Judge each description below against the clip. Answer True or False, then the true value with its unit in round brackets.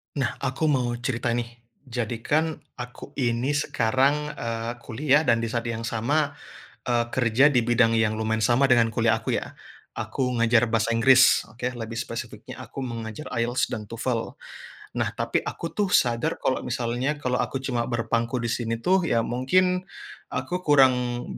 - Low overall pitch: True (120 Hz)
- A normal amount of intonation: False (2.3 semitones)